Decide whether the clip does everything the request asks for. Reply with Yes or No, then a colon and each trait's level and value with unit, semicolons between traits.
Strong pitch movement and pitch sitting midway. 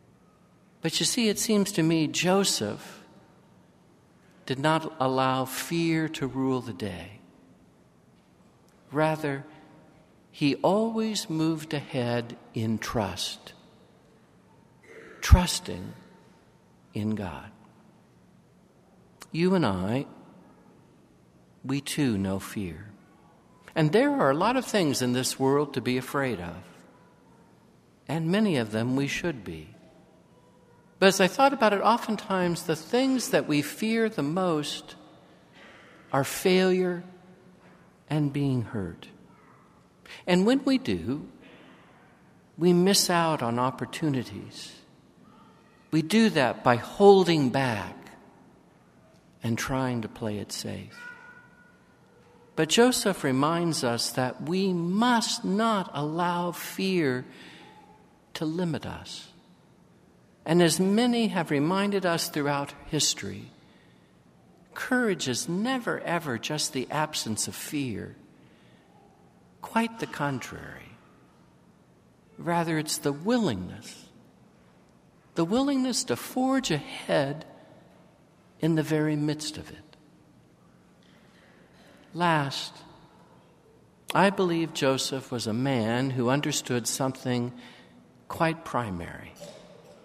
Yes: wide, 6.3 semitones; medium, 155 Hz